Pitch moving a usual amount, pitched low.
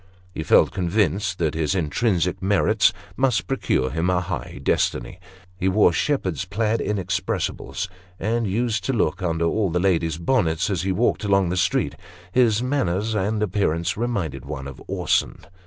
Yes: average, 4.2 semitones; very low, 95 Hz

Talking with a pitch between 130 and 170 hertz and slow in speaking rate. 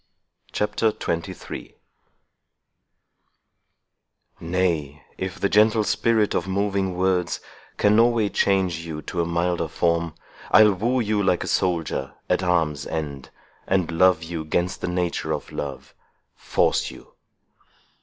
No: very low, 90 Hz; slow, 125 wpm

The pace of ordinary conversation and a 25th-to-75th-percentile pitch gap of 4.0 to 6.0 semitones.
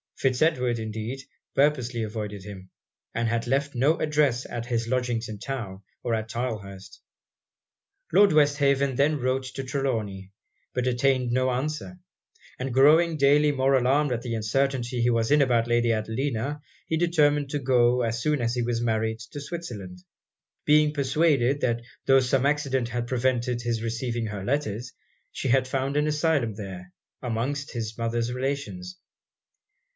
No: average, 155 wpm; average, 3.4 semitones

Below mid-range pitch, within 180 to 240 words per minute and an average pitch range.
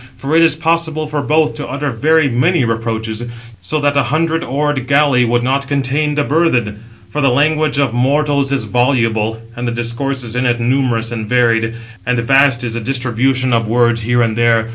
Yes: low, 130 Hz; fast, 205 wpm; average, 3.8 semitones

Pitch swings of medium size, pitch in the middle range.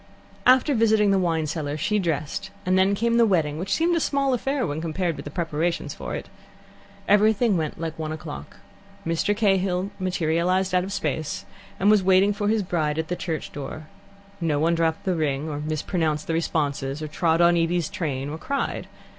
Yes: average, 4.2 semitones; medium, 170 Hz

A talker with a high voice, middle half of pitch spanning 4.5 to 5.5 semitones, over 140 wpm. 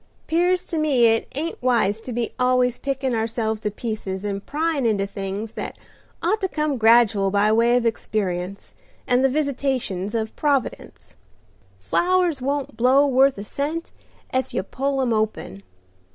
Yes: high, 245 Hz; average, 4.8 semitones; average, 155 wpm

